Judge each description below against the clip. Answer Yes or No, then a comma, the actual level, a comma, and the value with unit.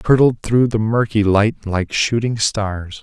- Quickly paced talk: No, average, 180 wpm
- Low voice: Yes, low, 110 Hz